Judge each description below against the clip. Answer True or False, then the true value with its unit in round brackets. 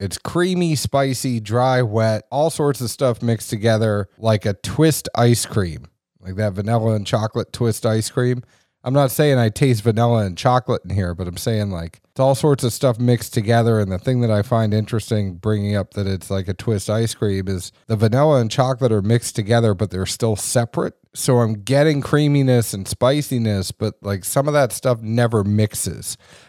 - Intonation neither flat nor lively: True (3.2 semitones)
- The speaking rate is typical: True (195 wpm)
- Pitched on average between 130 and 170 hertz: False (115 Hz)